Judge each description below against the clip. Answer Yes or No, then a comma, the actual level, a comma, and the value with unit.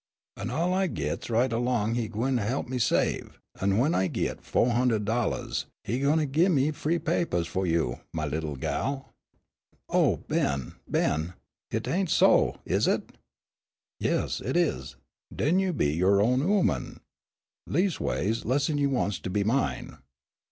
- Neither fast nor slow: Yes, average, 160 wpm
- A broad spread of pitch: Yes, wide, 7.1 semitones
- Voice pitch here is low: Yes, low, 120 Hz